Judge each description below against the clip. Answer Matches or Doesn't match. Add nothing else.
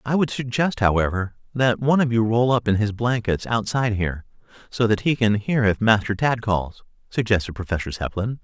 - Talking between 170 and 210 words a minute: Matches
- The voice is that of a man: Matches